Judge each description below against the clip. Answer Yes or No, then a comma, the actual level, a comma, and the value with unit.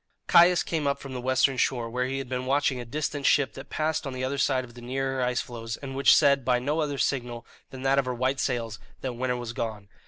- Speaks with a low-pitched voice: Yes, low, 130 Hz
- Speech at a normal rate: No, fast, 255 wpm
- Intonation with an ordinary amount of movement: No, narrow, 2.0 semitones